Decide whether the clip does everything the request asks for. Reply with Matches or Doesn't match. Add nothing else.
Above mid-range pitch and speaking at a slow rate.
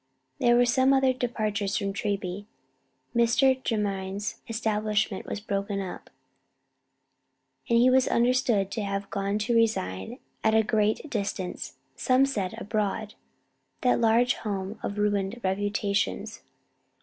Matches